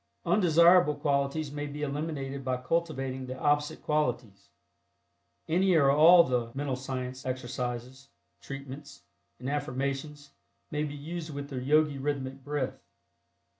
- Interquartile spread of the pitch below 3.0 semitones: Yes, narrow, 2.4 semitones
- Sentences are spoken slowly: Yes, slow, 125 wpm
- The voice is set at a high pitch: No, medium, 140 Hz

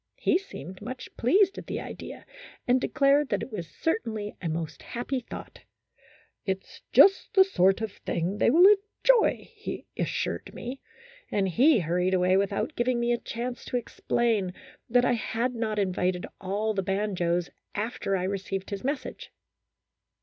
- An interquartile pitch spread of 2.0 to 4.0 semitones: No, average, 5.0 semitones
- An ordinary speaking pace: Yes, average, 160 wpm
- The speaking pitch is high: Yes, high, 220 Hz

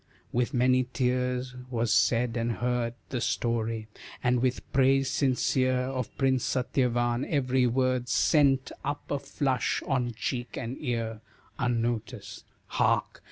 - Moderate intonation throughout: No, narrow, 1.6 semitones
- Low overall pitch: Yes, low, 125 Hz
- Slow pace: Yes, slow, 125 wpm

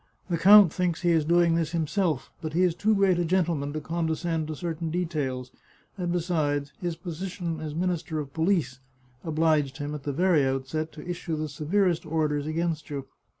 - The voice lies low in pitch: No, medium, 160 Hz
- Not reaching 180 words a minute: No, average, 185 wpm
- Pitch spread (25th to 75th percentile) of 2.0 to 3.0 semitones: Yes, narrow, 2.5 semitones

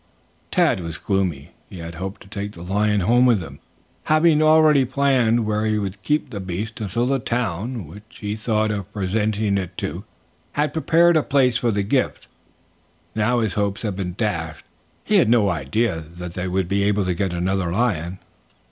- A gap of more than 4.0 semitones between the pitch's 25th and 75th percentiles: Yes, average, 4.4 semitones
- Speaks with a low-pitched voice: Yes, low, 105 Hz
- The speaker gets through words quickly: No, average, 185 wpm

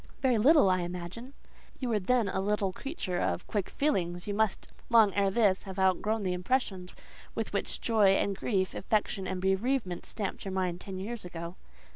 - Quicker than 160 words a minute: Yes, average, 180 wpm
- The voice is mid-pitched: No, high, 195 Hz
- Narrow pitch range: No, average, 3.3 semitones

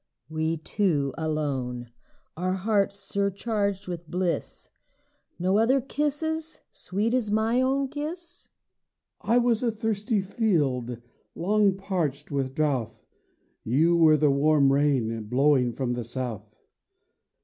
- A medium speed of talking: No, slow, 120 wpm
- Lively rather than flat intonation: Yes, wide, 7.8 semitones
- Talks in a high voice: No, medium, 175 Hz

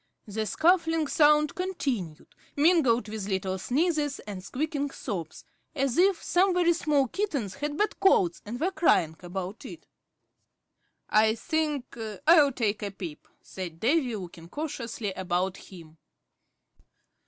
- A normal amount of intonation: No, wide, 8.6 semitones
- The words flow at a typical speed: No, slow, 130 wpm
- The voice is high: Yes, very high, 250 Hz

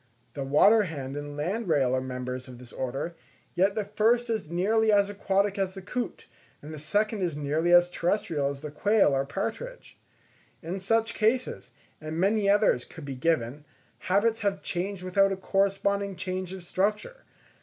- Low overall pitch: No, medium, 185 Hz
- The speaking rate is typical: Yes, average, 170 wpm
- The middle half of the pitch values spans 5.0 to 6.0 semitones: Yes, wide, 5.6 semitones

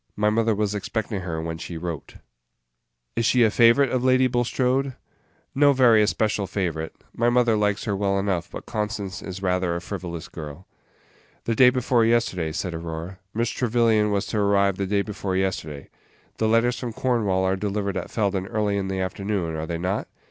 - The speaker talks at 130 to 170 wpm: No, average, 185 wpm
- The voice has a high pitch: No, low, 100 Hz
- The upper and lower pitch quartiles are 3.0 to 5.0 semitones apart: Yes, average, 3.7 semitones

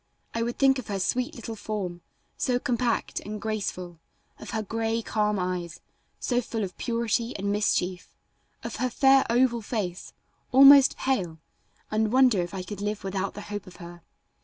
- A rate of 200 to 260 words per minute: No, average, 170 wpm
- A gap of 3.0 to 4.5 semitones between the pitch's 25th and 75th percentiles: Yes, average, 4.0 semitones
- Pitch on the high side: Yes, high, 215 Hz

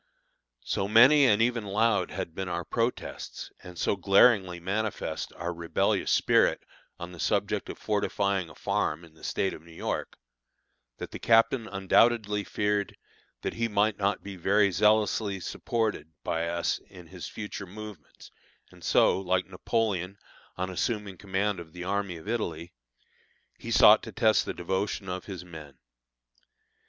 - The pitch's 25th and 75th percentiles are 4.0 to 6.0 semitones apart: No, average, 3.1 semitones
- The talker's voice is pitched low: Yes, low, 100 Hz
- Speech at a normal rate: Yes, average, 155 wpm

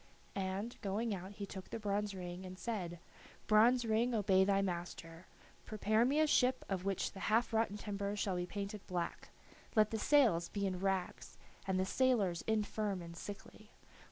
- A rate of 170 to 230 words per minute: Yes, average, 175 wpm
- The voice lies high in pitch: Yes, high, 200 Hz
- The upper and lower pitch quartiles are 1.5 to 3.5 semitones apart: Yes, average, 2.8 semitones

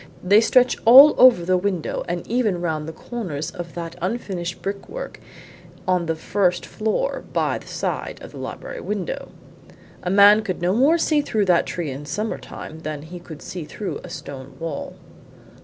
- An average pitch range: Yes, average, 4.7 semitones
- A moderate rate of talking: Yes, average, 175 wpm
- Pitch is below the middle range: No, medium, 180 Hz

